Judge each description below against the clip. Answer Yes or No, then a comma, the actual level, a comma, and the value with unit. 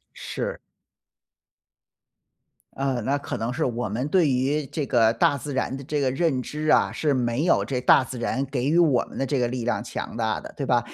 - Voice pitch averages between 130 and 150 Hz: Yes, low, 135 Hz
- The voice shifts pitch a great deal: No, average, 3.0 semitones